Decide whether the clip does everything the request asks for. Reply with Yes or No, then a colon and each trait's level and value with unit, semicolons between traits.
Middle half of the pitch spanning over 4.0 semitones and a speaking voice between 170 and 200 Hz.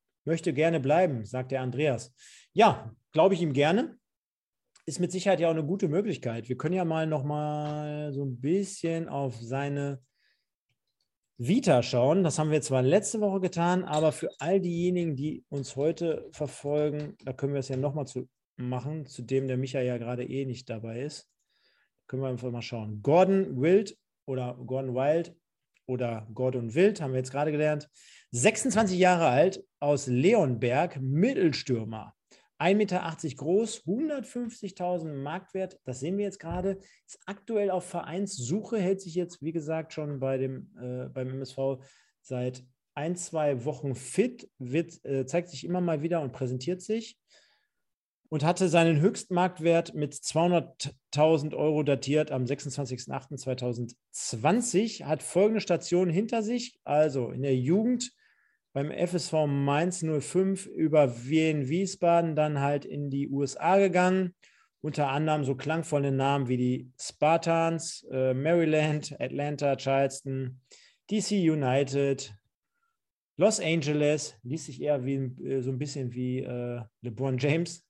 No: average, 5.0 semitones; medium, 150 Hz